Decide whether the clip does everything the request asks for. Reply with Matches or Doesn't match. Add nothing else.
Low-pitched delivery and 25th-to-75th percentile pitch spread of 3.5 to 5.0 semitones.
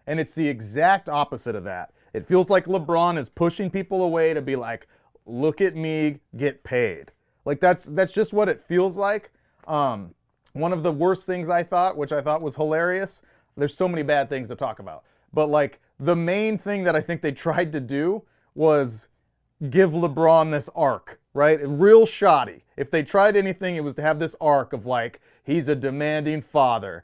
Doesn't match